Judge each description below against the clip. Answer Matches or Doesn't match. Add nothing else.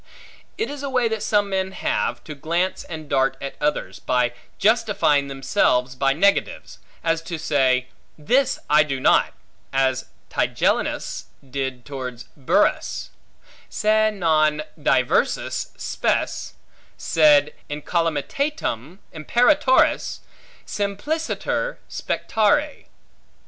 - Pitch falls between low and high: Matches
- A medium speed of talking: Doesn't match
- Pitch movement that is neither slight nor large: Doesn't match